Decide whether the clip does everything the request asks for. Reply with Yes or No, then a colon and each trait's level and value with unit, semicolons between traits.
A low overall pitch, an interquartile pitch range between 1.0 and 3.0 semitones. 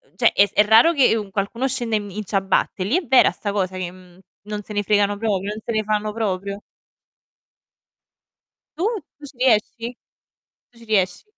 No: high, 210 Hz; narrow, 2.6 semitones